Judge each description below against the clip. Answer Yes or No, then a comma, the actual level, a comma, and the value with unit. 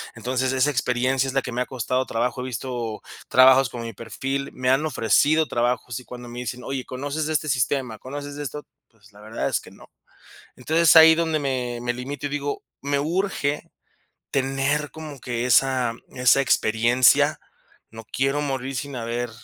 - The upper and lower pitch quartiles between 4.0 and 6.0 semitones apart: No, average, 2.7 semitones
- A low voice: Yes, low, 130 Hz